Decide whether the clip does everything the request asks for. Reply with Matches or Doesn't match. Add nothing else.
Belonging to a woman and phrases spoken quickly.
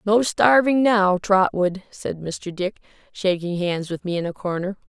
Doesn't match